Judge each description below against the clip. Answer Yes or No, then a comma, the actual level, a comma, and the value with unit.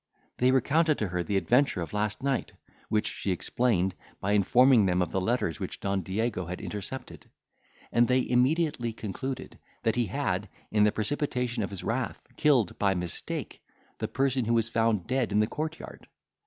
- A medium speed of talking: Yes, average, 180 wpm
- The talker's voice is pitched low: Yes, low, 115 Hz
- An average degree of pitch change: Yes, average, 4.6 semitones